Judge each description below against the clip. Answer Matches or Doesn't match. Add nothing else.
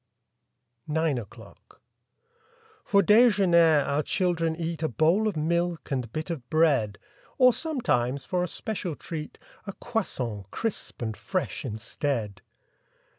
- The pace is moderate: Doesn't match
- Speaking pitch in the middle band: Matches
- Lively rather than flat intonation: Matches